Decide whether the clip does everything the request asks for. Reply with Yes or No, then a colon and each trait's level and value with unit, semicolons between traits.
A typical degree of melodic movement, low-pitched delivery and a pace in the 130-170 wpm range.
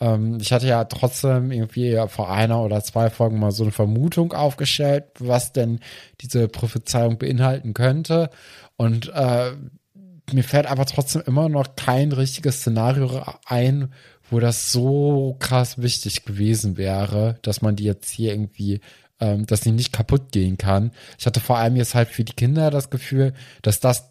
Yes: average, 3.1 semitones; low, 120 Hz; average, 165 wpm